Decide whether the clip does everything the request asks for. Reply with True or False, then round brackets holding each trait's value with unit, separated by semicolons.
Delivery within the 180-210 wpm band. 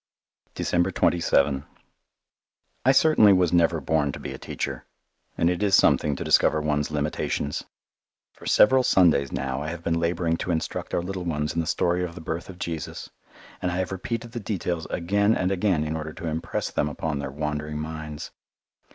True (185 wpm)